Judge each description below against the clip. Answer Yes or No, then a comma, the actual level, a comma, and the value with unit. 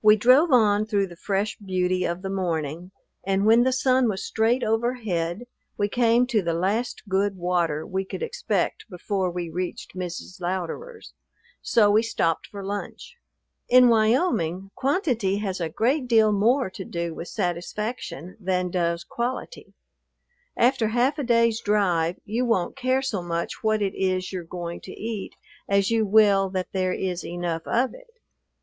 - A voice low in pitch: No, high, 200 Hz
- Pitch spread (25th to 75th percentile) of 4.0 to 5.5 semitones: Yes, average, 4.4 semitones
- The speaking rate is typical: Yes, average, 165 wpm